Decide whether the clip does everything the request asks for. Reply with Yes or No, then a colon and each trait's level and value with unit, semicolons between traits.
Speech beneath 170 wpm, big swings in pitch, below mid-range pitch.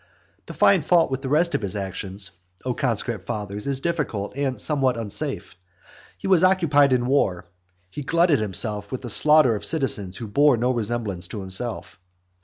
No: average, 175 wpm; wide, 6.0 semitones; low, 125 Hz